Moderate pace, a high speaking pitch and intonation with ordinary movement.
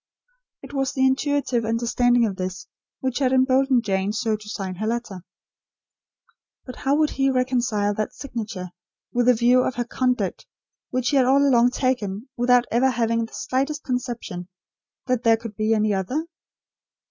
Yes: average, 165 wpm; high, 245 Hz; average, 3.2 semitones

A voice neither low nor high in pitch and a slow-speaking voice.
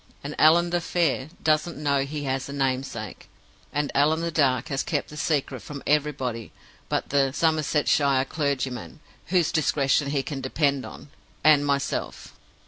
No: medium, 145 Hz; average, 150 wpm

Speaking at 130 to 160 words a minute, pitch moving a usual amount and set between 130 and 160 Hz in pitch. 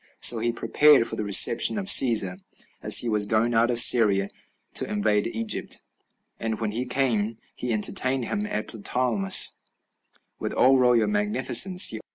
No: average, 155 wpm; average, 3.4 semitones; low, 115 Hz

